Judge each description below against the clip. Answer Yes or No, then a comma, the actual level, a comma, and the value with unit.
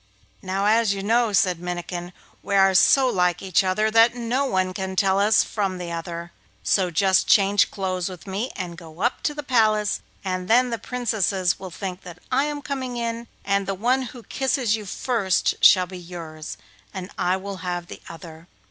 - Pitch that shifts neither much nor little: Yes, average, 4.1 semitones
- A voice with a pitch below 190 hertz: No, high, 195 Hz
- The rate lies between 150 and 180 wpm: No, average, 200 wpm